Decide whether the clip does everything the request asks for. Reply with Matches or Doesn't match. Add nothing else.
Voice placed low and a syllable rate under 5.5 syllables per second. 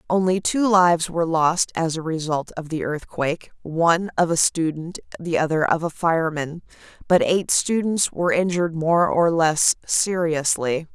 Doesn't match